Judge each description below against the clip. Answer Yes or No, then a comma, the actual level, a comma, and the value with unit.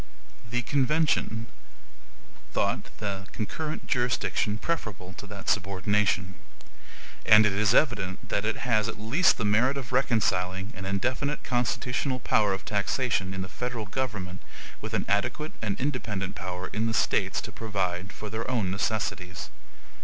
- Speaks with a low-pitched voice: Yes, low, 105 Hz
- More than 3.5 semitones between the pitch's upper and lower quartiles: Yes, average, 4.1 semitones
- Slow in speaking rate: No, average, 145 wpm